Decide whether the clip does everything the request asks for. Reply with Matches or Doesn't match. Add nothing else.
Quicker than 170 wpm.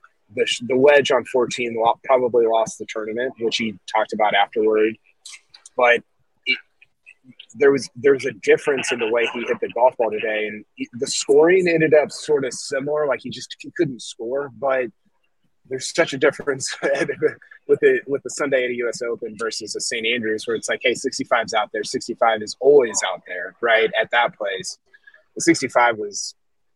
Matches